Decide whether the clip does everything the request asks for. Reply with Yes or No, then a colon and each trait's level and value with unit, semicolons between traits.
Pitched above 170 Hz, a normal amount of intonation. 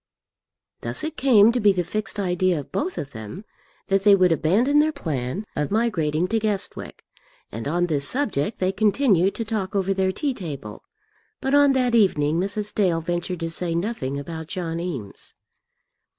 Yes: high, 190 Hz; average, 4.8 semitones